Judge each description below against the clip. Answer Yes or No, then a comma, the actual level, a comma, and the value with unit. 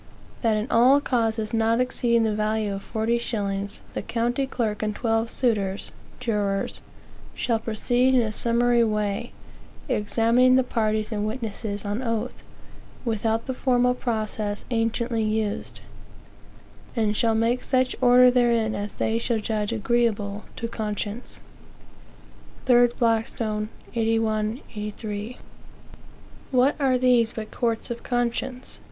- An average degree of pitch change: No, narrow, 2.2 semitones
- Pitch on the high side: Yes, high, 225 Hz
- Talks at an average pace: No, slow, 125 wpm